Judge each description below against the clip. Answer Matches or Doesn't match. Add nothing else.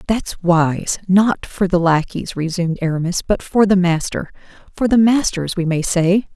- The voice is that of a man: Doesn't match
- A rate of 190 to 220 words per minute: Doesn't match